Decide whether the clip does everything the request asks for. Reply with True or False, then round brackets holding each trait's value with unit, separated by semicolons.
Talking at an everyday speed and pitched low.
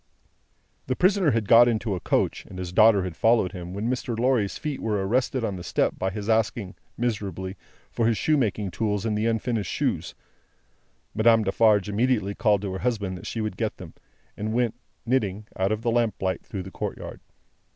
True (190 wpm; 110 Hz)